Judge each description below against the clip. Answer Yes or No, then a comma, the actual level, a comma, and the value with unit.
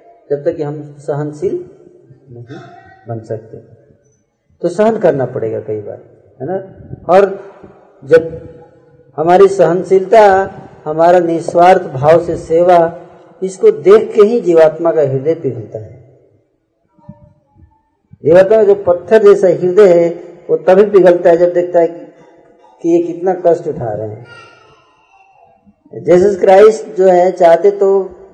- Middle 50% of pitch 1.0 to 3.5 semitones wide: Yes, average, 3.2 semitones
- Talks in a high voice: No, medium, 175 Hz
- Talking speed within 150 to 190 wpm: No, average, 130 wpm